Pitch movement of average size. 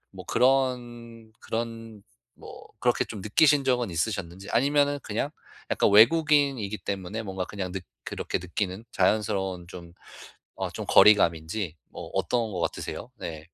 Yes: average, 4.6 semitones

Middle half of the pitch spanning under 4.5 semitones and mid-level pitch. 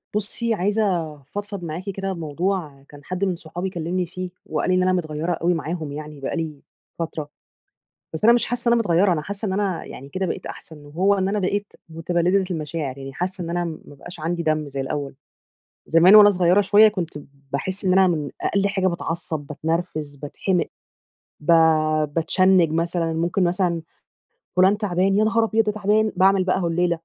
Yes: average, 3.4 semitones; medium, 175 Hz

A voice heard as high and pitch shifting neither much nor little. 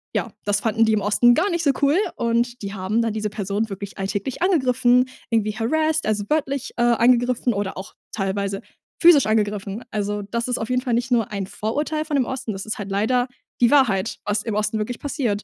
Yes: high, 225 Hz; average, 3.6 semitones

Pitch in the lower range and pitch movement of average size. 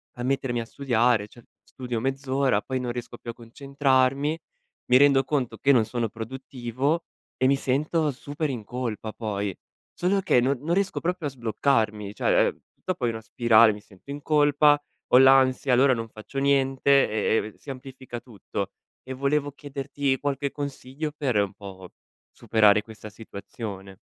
Yes: low, 130 Hz; average, 3.7 semitones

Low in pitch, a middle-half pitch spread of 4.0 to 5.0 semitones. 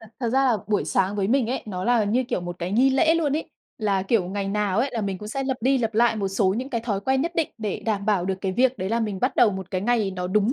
No: high, 215 Hz; average, 4.3 semitones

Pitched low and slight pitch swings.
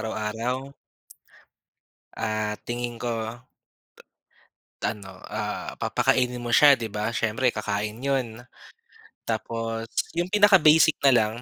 No: low, 115 Hz; average, 3.2 semitones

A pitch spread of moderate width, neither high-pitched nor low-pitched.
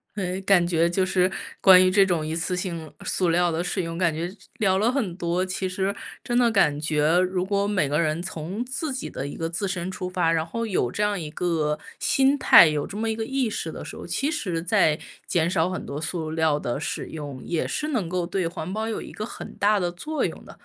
Yes: average, 3.6 semitones; medium, 180 Hz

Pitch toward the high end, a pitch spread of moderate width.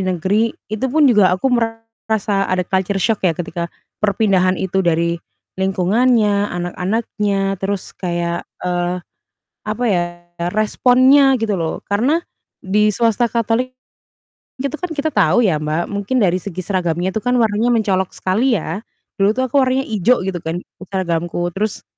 Yes: high, 200 Hz; average, 4.0 semitones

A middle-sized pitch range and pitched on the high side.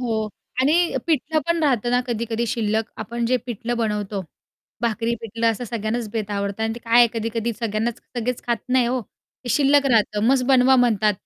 No: narrow, 2.2 semitones; high, 235 Hz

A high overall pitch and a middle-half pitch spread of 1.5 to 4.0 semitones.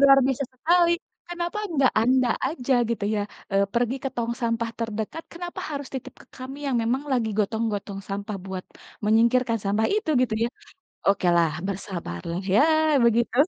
No: high, 235 Hz; average, 4.4 semitones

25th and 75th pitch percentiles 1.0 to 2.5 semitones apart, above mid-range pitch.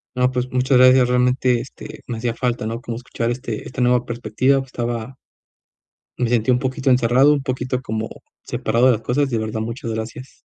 No: narrow, 1.7 semitones; low, 125 Hz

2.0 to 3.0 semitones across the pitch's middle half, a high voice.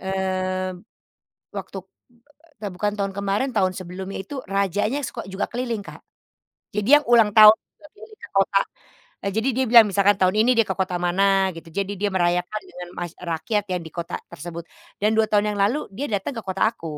Yes: narrow, 2.5 semitones; high, 195 Hz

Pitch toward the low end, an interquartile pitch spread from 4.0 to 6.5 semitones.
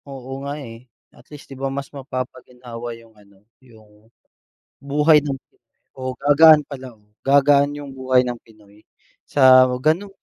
No: low, 130 Hz; average, 2.9 semitones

